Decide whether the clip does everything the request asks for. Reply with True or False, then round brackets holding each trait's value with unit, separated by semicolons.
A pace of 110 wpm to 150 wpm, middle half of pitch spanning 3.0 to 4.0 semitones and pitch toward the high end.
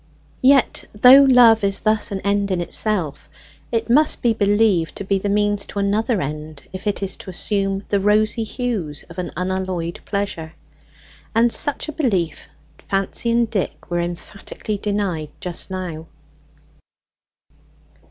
True (145 wpm; 3.3 semitones; 200 Hz)